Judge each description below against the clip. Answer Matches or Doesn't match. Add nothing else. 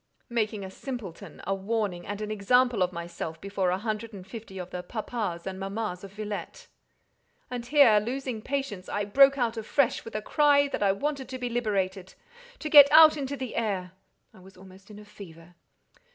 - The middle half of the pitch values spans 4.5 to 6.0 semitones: Matches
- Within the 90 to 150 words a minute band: Doesn't match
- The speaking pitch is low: Doesn't match